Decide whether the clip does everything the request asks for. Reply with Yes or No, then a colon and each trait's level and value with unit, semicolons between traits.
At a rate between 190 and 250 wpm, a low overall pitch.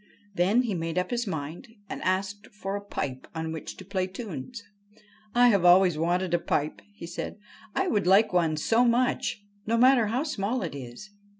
No: average, 200 wpm; high, 195 Hz